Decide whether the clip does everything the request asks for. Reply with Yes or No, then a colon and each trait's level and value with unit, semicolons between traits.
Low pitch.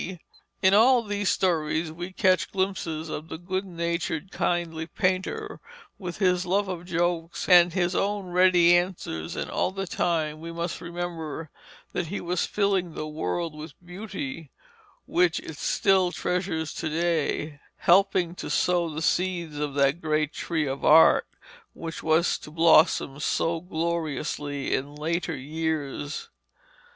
No: medium, 170 Hz